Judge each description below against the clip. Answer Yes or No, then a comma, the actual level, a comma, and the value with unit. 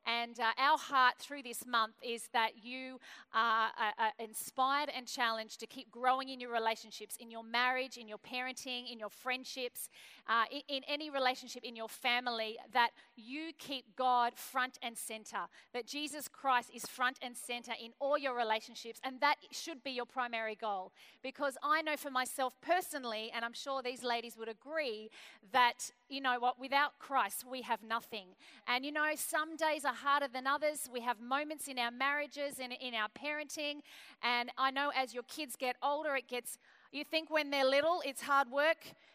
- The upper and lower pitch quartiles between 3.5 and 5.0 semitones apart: No, average, 3.1 semitones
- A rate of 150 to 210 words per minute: Yes, average, 190 wpm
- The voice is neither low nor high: No, very high, 255 Hz